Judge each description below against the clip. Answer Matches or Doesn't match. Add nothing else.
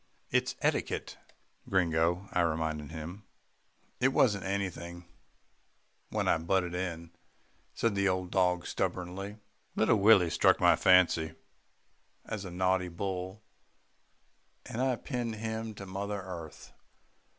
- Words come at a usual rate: Doesn't match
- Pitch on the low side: Matches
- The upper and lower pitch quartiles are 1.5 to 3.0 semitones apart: Matches